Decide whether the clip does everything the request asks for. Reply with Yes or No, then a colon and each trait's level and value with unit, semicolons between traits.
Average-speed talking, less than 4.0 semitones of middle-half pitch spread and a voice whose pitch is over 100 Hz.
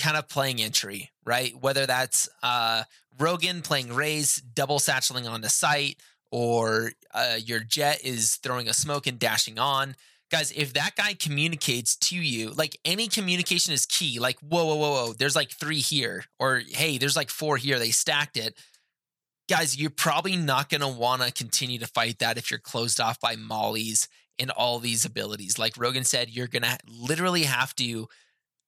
No: average, 180 wpm; average, 4.3 semitones; low, 135 Hz